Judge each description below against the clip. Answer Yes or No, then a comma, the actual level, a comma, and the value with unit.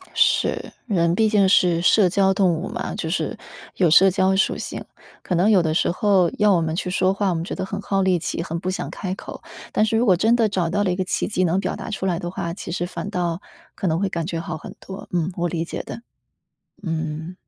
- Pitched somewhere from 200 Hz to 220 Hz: No, medium, 185 Hz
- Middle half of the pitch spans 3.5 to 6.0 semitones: No, average, 2.7 semitones